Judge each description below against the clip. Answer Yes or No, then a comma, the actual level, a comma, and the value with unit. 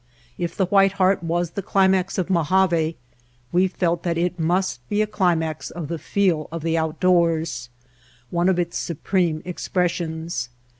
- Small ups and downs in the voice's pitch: Yes, narrow, 2.3 semitones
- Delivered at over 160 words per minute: No, average, 155 wpm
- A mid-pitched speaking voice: Yes, medium, 175 Hz